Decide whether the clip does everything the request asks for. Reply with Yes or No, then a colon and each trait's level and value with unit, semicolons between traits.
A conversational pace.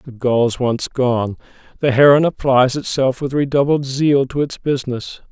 Yes: average, 160 wpm